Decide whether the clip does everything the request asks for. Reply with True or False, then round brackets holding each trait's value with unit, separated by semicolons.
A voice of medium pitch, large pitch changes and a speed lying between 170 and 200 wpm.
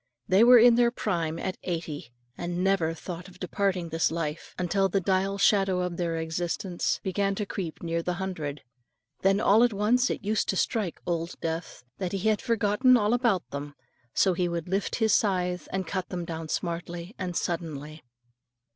False (180 Hz; 3.1 semitones; 180 wpm)